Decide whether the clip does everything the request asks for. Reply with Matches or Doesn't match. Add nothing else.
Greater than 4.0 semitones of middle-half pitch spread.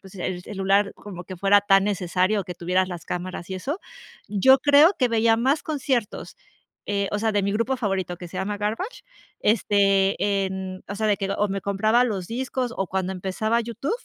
Doesn't match